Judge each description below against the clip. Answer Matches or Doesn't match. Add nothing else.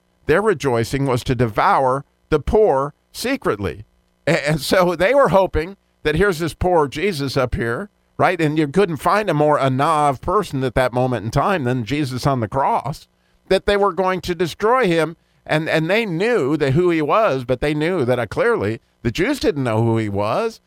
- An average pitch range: Doesn't match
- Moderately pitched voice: Matches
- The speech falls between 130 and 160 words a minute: Doesn't match